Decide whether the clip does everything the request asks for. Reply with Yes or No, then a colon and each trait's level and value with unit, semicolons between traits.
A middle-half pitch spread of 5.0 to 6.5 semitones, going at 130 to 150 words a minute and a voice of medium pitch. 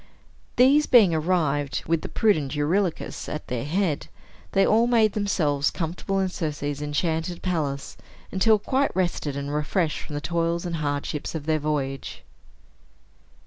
No: average, 4.6 semitones; average, 145 wpm; medium, 165 Hz